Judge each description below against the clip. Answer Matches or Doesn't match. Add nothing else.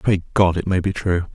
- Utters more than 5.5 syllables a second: Doesn't match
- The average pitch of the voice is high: Doesn't match